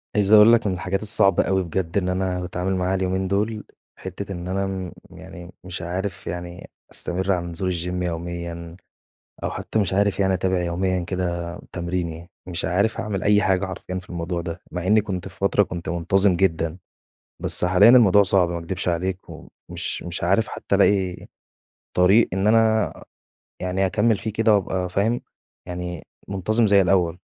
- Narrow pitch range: Yes, narrow, 2.1 semitones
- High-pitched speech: No, very low, 95 Hz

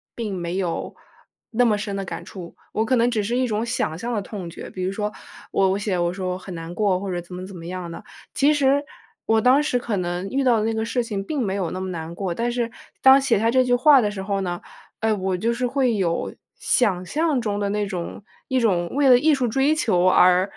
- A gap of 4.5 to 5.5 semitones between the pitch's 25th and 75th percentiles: Yes, average, 4.9 semitones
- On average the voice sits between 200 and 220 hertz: Yes, high, 210 Hz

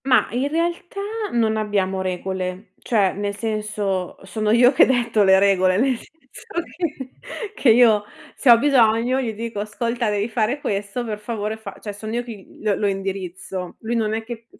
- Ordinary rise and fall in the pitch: Yes, average, 3.2 semitones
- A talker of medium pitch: No, high, 220 Hz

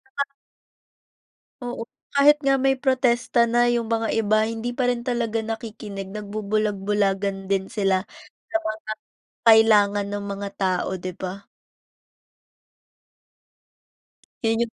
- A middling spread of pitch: Yes, average, 3.0 semitones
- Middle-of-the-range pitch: No, high, 215 Hz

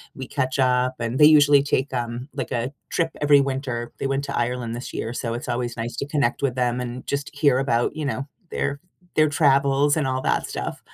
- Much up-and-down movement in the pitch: No, narrow, 2.6 semitones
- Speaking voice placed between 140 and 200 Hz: No, low, 130 Hz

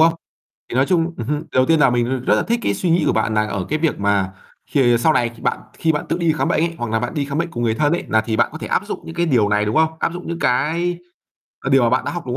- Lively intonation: Yes, wide, 5.8 semitones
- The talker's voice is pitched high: No, medium, 140 Hz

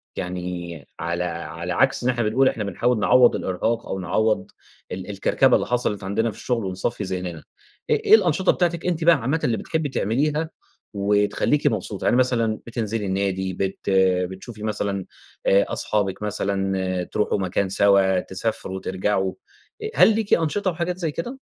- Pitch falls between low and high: No, low, 105 Hz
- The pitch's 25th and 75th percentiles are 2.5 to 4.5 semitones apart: No, average, 5.1 semitones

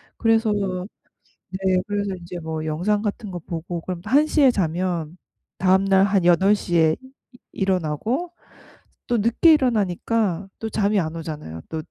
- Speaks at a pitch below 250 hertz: Yes, high, 190 Hz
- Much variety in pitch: No, average, 4.0 semitones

